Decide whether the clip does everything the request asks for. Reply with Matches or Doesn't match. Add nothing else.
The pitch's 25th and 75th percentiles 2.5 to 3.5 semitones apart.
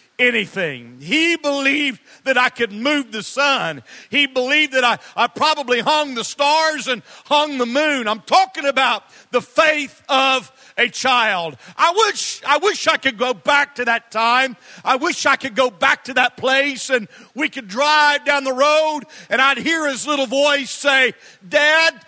Matches